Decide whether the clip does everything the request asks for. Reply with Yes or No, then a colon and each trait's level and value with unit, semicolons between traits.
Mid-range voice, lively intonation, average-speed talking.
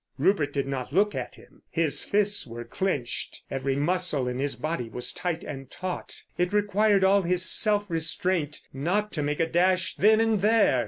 Yes: medium, 175 Hz; wide, 6.0 semitones; average, 180 wpm